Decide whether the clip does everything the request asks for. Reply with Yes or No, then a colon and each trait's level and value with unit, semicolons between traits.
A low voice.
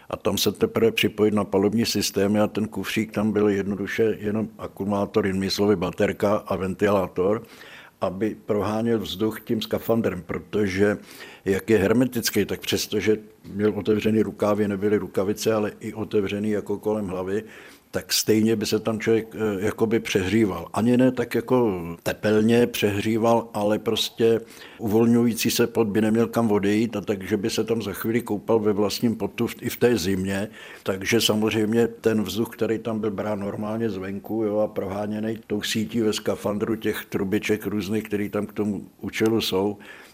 Yes: low, 105 Hz